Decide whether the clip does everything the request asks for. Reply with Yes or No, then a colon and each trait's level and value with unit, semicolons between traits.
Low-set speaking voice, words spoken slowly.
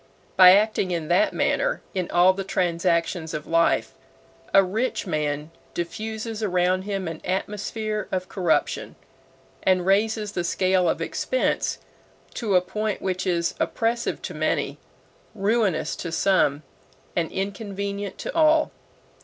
No: high, 190 Hz; slow, 130 wpm